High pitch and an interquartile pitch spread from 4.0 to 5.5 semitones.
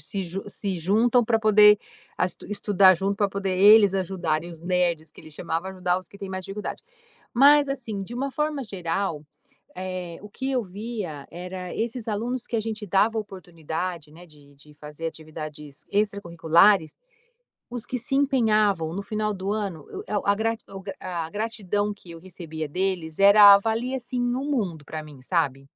Yes: high, 195 Hz; average, 4.4 semitones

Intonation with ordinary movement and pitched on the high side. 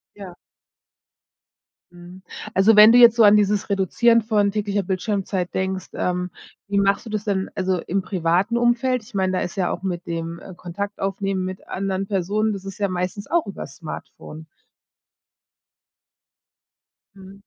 No: narrow, 2.2 semitones; high, 195 Hz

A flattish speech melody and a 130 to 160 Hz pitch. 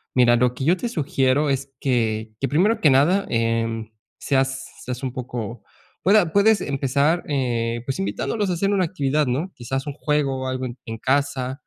No: average, 3.6 semitones; low, 135 Hz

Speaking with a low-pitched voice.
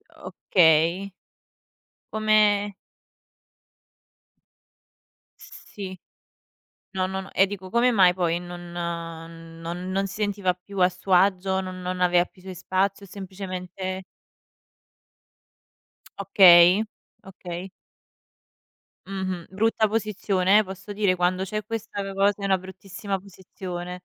No: high, 190 Hz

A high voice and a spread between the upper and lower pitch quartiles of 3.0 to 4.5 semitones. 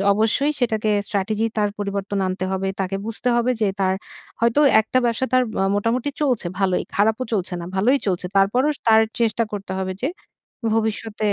Yes: high, 215 Hz; average, 3.3 semitones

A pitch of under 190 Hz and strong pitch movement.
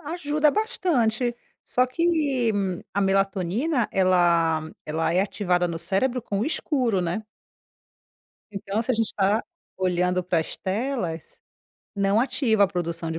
No: high, 200 Hz; wide, 6.0 semitones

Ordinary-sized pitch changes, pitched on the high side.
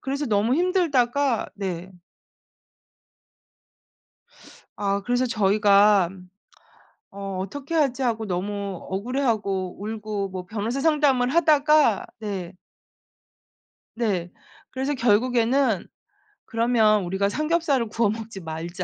Yes: average, 5.0 semitones; high, 220 Hz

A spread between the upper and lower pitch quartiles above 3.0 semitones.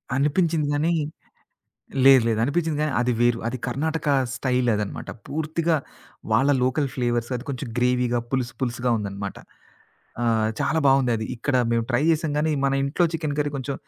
Yes: average, 3.8 semitones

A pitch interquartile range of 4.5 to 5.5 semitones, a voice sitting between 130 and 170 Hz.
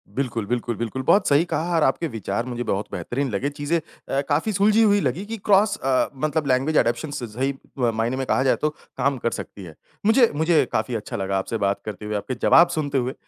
Yes: average, 5.2 semitones; low, 135 Hz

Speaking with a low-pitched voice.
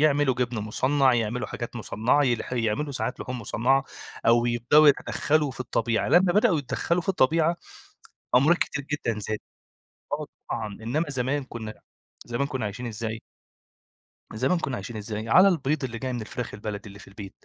Yes: low, 125 Hz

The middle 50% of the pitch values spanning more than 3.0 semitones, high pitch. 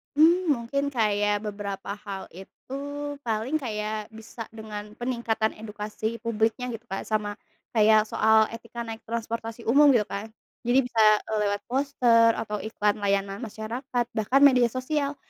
No: narrow, 2.4 semitones; high, 225 Hz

